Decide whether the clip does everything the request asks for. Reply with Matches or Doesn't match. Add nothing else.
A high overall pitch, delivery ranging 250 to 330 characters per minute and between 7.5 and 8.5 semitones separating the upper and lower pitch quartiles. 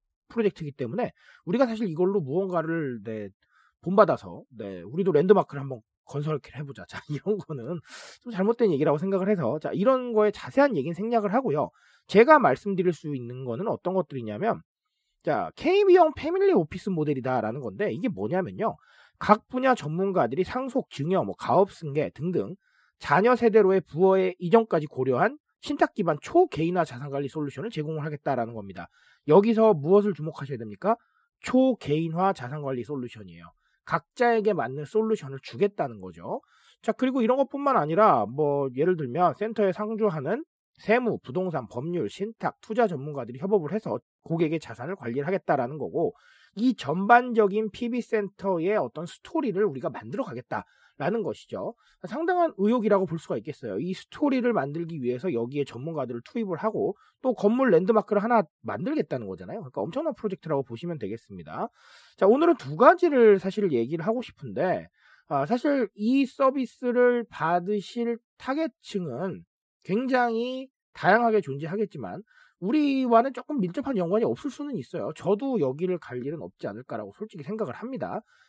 Doesn't match